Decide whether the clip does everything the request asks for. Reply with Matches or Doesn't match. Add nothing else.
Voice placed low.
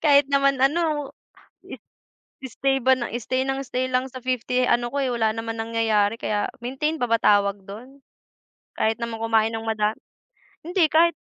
Doesn't match